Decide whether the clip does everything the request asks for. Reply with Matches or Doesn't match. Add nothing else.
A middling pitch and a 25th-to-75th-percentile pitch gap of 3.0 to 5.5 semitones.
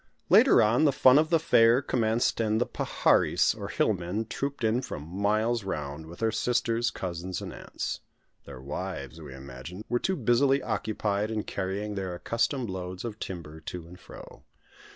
Doesn't match